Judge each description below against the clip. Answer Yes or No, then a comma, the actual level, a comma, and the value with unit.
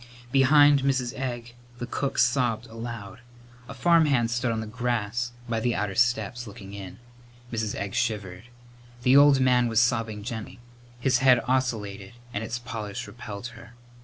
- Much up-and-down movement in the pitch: No, narrow, 2.6 semitones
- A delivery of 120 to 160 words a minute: Yes, average, 155 wpm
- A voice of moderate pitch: No, low, 120 Hz